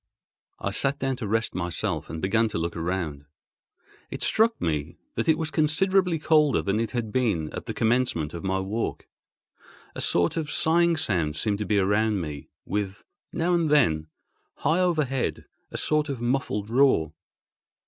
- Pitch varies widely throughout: Yes, wide, 8.3 semitones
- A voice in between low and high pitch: No, low, 115 Hz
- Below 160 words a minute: No, average, 165 wpm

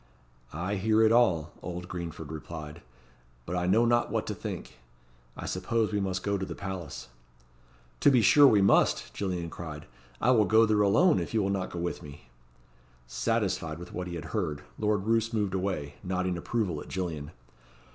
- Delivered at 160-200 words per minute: Yes, average, 185 wpm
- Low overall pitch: Yes, very low, 95 Hz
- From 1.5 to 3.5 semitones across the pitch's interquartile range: No, average, 4.3 semitones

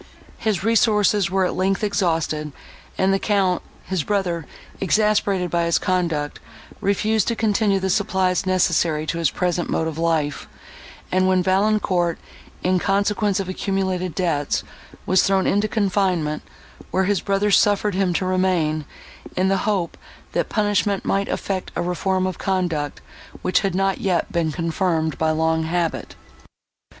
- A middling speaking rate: Yes, average, 145 wpm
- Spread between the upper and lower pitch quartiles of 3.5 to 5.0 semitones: No, average, 2.8 semitones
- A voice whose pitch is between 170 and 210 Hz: Yes, medium, 185 Hz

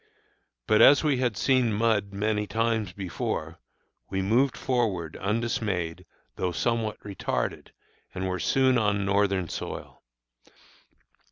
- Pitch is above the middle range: No, low, 105 Hz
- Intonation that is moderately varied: Yes, average, 3.5 semitones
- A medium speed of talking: No, slow, 115 wpm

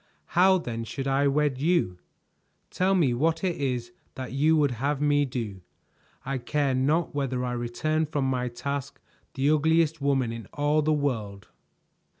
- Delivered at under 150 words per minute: No, average, 160 wpm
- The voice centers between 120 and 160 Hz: Yes, medium, 140 Hz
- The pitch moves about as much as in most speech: Yes, average, 3.5 semitones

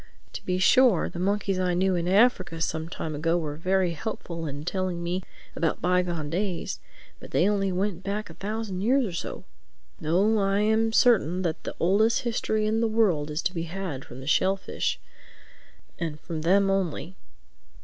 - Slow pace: No, average, 175 wpm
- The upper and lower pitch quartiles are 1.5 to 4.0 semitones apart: Yes, average, 3.5 semitones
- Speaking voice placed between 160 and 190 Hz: Yes, medium, 185 Hz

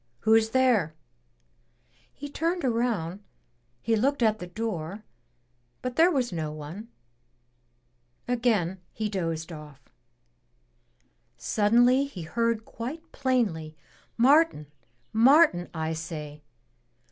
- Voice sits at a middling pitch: No, high, 220 Hz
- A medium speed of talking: No, slow, 100 wpm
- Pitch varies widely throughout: Yes, wide, 7.5 semitones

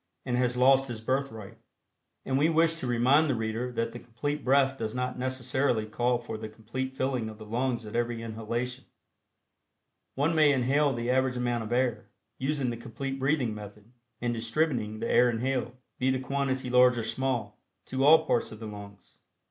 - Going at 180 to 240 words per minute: Yes, average, 185 wpm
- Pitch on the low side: Yes, low, 125 Hz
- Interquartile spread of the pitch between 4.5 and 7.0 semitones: No, narrow, 2.6 semitones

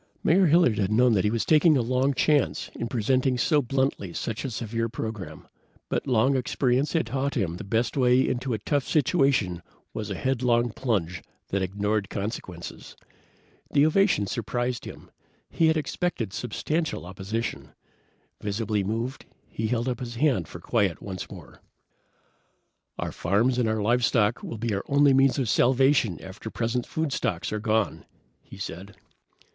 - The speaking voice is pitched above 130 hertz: No, low, 120 Hz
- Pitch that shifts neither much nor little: Yes, average, 4.3 semitones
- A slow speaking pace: No, average, 160 wpm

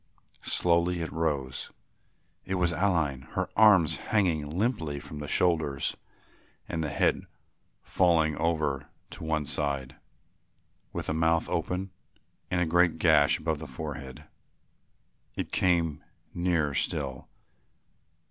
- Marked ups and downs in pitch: No, average, 3.0 semitones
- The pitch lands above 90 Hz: No, very low, 80 Hz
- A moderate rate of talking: No, slow, 120 wpm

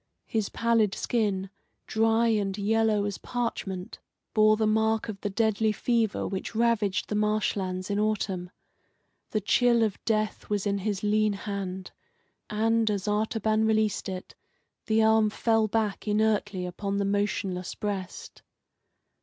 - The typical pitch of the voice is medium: No, high, 210 Hz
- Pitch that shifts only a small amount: Yes, narrow, 1.7 semitones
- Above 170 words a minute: No, average, 140 wpm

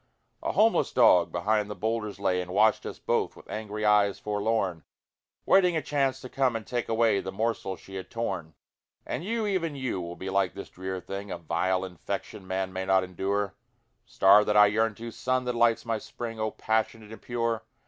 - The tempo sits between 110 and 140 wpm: No, average, 200 wpm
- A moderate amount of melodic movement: Yes, average, 3.5 semitones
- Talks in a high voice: No, low, 105 Hz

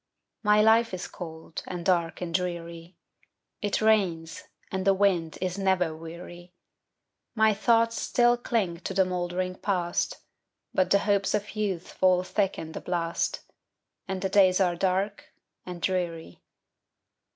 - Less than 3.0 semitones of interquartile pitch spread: Yes, narrow, 2.6 semitones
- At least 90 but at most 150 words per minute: Yes, average, 140 wpm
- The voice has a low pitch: No, medium, 185 Hz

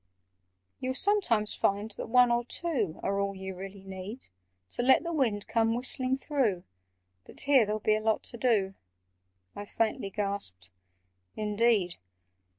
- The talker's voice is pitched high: Yes, high, 215 Hz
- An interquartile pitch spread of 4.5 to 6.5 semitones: No, average, 3.9 semitones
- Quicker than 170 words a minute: No, average, 150 wpm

